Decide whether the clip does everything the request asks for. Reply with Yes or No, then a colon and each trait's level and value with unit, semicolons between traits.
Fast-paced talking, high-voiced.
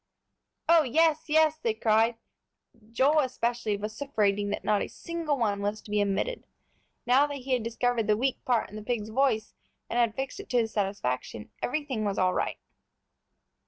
No: average, 175 wpm; high, 235 Hz